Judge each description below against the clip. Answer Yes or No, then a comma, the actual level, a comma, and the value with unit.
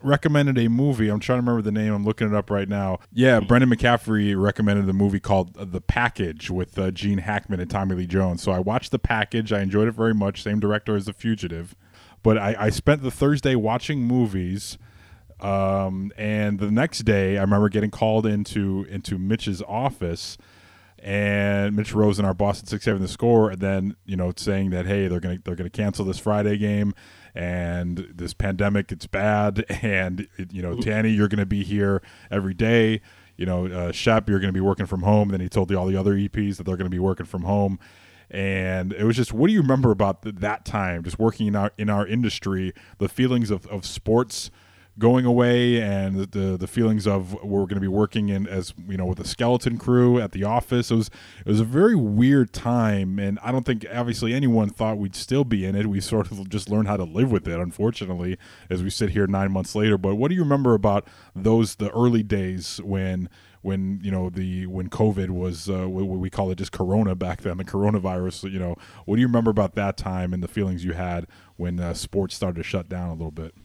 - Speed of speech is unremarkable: No, fast, 225 wpm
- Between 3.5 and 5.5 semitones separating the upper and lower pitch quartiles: No, narrow, 2.6 semitones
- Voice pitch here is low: Yes, low, 100 Hz